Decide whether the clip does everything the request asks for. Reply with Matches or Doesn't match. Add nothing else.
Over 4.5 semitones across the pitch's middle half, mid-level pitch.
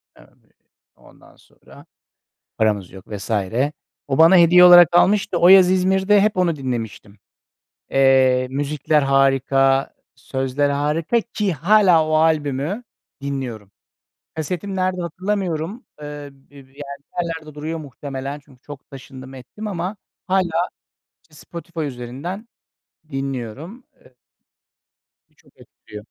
Matches